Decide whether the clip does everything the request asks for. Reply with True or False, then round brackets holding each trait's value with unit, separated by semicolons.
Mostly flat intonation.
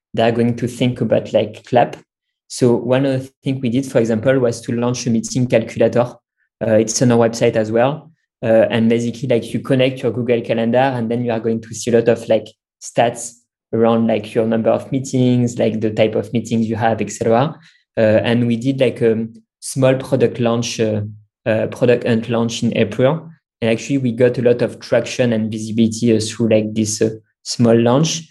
True (1.8 semitones)